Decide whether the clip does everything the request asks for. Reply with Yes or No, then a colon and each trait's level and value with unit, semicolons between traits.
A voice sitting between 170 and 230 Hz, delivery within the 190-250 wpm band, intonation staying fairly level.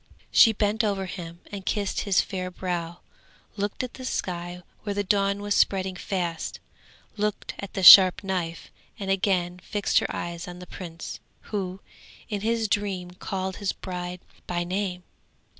No: high, 190 Hz; average, 160 wpm; narrow, 2.2 semitones